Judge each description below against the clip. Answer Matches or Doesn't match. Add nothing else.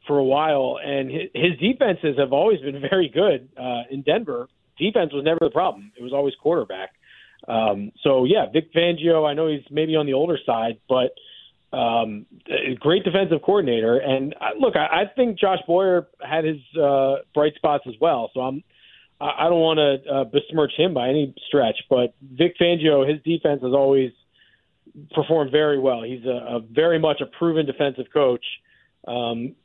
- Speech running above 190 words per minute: Doesn't match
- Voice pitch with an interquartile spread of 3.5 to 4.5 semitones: Matches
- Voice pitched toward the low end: Doesn't match